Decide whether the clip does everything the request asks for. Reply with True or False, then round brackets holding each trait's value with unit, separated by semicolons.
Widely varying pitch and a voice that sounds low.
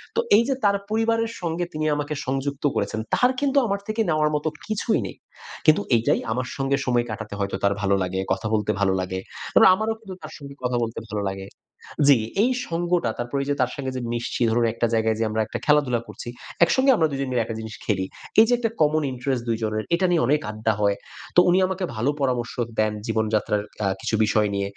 True (7.5 semitones; 130 Hz)